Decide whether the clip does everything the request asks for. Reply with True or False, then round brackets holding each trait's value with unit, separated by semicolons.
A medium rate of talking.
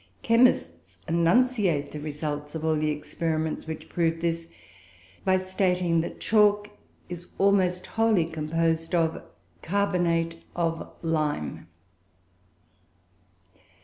False (100 wpm)